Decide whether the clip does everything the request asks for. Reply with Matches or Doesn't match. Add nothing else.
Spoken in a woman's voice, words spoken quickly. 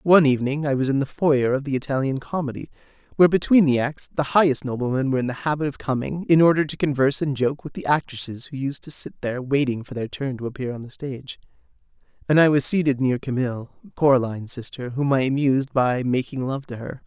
Doesn't match